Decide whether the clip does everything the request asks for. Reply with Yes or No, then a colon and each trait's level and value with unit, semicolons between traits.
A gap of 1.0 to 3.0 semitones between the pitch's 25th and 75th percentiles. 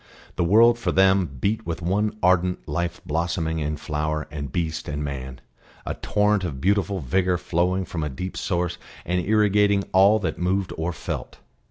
No: average, 3.6 semitones